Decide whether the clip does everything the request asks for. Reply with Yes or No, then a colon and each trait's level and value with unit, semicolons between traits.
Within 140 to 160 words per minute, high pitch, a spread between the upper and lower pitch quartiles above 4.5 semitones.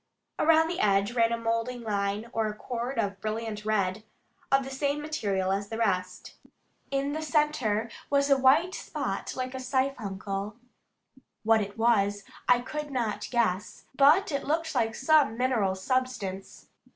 Yes: average, 150 wpm; high, 230 Hz; average, 5.0 semitones